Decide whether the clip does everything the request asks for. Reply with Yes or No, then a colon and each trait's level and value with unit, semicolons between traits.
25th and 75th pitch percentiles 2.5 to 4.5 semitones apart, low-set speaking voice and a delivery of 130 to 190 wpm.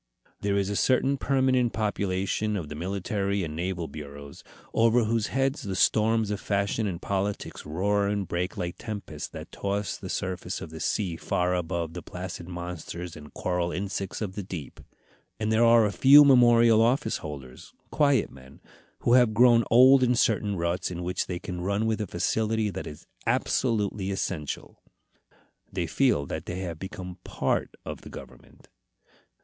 Yes: average, 4.2 semitones; low, 100 Hz; average, 170 wpm